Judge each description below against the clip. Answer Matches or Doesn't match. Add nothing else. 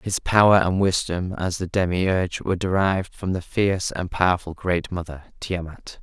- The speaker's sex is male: Matches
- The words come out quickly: Doesn't match